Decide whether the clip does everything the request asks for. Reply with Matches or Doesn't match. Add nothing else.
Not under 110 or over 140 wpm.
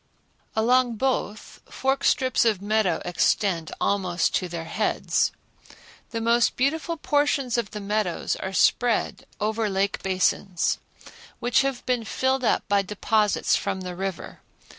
Matches